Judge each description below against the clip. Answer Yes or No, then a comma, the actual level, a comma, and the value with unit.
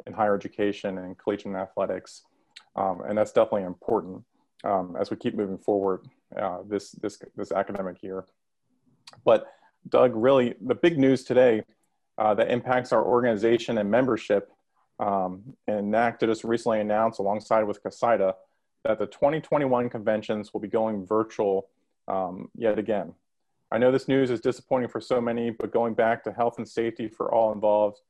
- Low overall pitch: Yes, low, 110 Hz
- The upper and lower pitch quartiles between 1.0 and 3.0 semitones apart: Yes, narrow, 2.6 semitones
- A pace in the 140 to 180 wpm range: Yes, average, 160 wpm